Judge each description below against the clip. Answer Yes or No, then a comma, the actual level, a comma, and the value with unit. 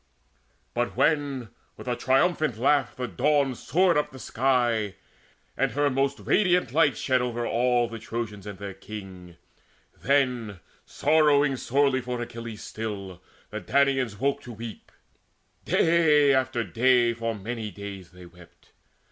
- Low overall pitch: Yes, low, 125 Hz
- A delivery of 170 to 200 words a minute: No, average, 140 wpm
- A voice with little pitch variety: No, average, 4.2 semitones